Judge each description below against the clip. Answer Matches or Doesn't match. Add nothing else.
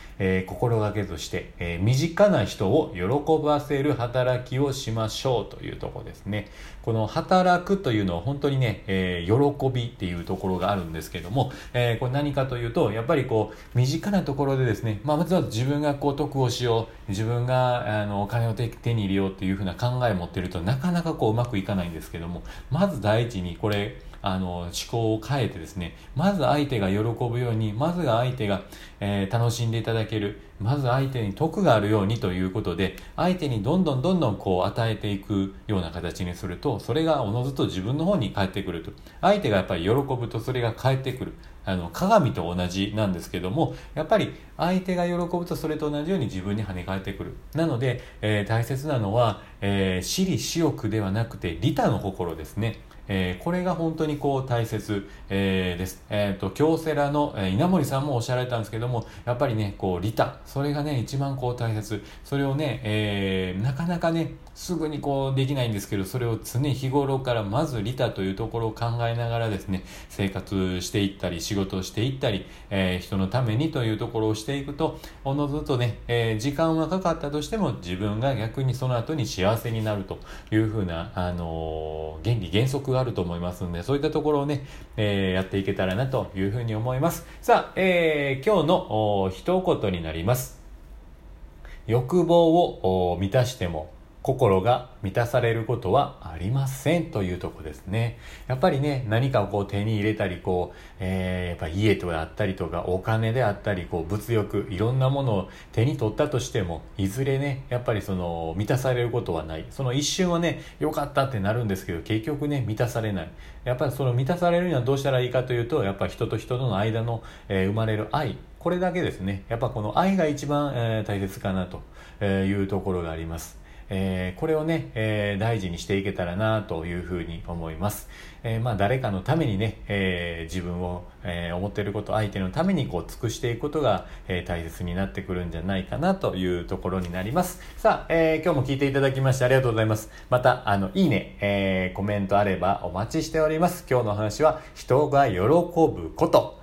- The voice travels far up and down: Matches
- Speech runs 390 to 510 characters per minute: Matches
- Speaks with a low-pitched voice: Matches